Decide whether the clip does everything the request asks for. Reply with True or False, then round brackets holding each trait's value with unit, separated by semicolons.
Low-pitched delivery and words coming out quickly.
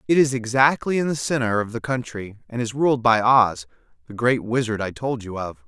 True (120 Hz; 220 wpm)